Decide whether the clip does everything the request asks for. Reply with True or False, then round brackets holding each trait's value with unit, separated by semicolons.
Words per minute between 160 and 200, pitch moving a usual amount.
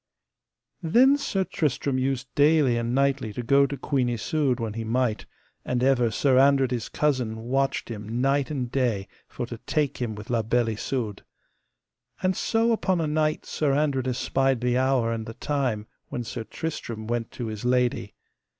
True (175 wpm; 3.2 semitones)